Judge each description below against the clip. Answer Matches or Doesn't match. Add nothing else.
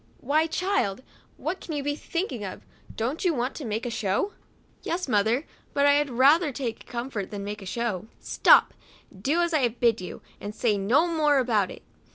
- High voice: Matches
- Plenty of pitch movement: Matches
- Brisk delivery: Matches